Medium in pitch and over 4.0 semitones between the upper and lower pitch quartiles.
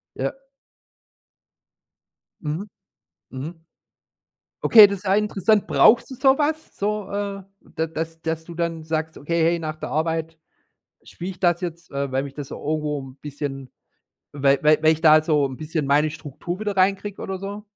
Yes: medium, 165 Hz; average, 4.5 semitones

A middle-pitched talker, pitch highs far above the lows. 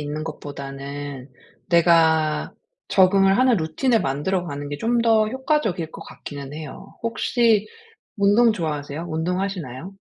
Yes: medium, 170 Hz; wide, 6.5 semitones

